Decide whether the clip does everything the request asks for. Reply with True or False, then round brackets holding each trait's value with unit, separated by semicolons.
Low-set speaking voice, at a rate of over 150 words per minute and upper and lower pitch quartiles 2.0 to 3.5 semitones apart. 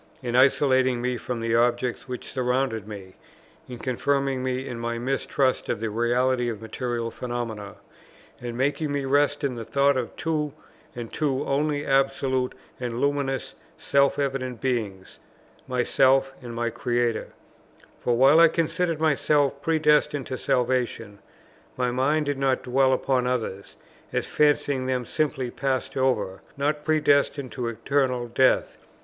False (130 Hz; 145 wpm; 2.6 semitones)